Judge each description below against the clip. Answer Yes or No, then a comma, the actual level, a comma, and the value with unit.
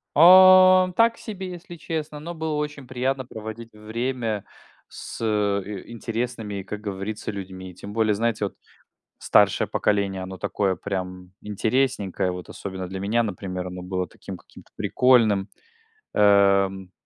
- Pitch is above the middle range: No, low, 105 Hz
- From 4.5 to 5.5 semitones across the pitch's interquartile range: Yes, average, 5.2 semitones